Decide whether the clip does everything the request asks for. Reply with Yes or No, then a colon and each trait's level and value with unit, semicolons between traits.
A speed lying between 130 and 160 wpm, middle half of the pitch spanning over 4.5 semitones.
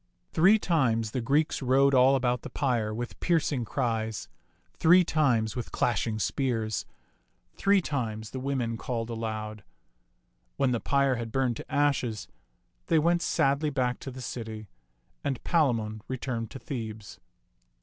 No: average, 145 wpm; average, 3.7 semitones